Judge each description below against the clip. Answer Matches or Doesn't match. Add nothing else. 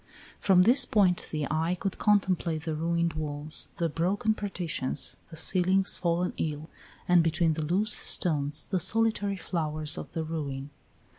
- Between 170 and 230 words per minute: Doesn't match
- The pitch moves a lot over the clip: Doesn't match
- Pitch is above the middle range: Doesn't match